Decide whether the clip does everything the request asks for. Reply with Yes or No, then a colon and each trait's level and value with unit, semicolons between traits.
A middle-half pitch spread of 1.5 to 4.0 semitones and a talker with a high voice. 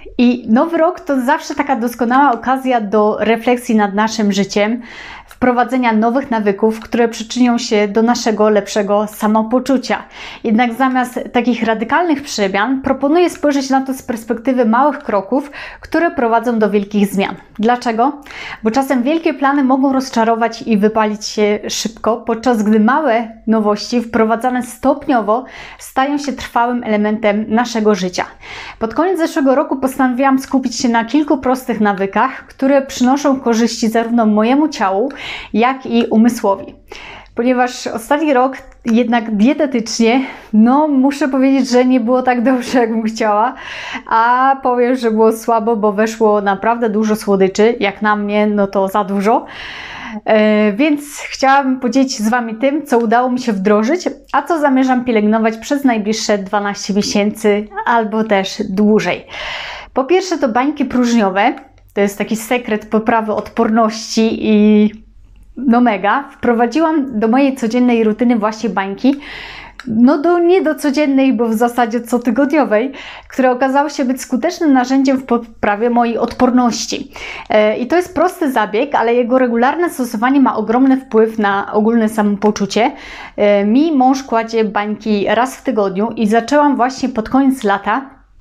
Yes: average, 3.5 semitones; high, 240 Hz